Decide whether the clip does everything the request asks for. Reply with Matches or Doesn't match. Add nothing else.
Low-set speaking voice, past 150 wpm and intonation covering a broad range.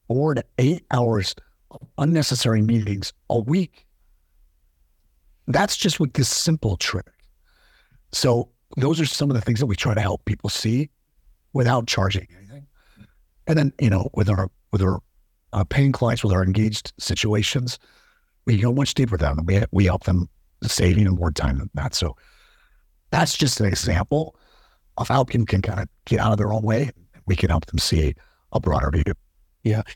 Matches